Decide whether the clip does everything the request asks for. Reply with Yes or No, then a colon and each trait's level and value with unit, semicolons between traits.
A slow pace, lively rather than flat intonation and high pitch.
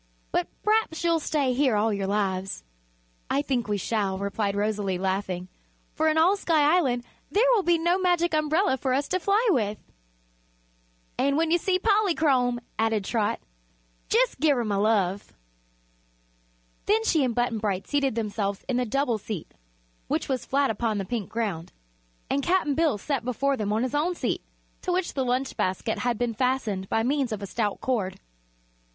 No: average, 175 wpm; wide, 7.0 semitones; very high, 250 Hz